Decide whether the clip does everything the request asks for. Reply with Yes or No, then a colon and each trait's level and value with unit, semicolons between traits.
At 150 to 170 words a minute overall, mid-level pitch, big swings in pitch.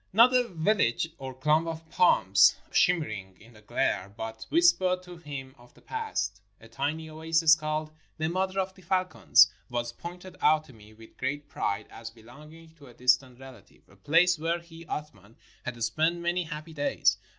No: average, 185 wpm; medium, 150 Hz; wide, 6.3 semitones